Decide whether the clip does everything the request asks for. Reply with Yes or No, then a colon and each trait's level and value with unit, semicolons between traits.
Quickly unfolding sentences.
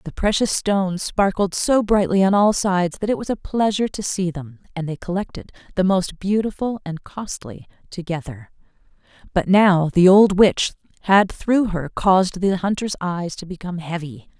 No: average, 170 wpm